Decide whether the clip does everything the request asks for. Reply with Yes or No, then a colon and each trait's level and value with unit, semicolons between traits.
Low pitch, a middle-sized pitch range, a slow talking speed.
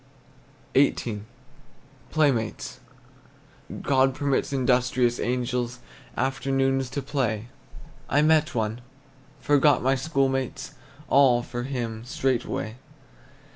No: low, 130 Hz; narrow, 2.1 semitones; slow, 90 wpm